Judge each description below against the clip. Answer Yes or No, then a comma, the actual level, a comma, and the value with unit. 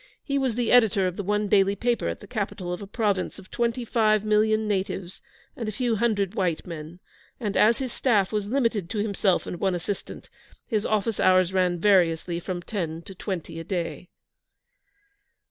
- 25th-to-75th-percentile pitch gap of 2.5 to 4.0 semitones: Yes, average, 3.1 semitones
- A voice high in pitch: Yes, high, 200 Hz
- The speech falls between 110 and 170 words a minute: No, average, 180 wpm